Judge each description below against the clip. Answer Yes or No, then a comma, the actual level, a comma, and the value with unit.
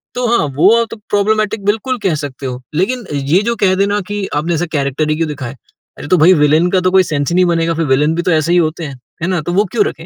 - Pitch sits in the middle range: Yes, medium, 170 Hz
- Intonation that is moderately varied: Yes, average, 4.8 semitones